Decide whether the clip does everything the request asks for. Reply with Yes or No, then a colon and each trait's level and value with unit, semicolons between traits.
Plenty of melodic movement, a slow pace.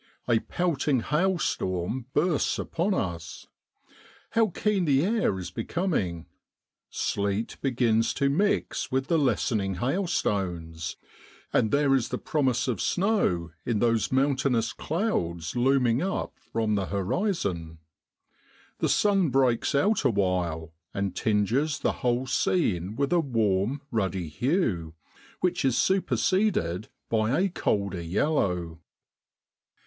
Yes: wide, 8.3 semitones; slow, 115 wpm